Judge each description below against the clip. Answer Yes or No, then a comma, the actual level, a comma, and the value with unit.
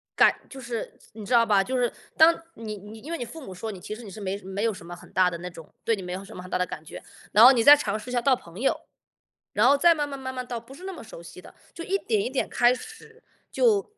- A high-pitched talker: Yes, high, 230 Hz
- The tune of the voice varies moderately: No, wide, 6.3 semitones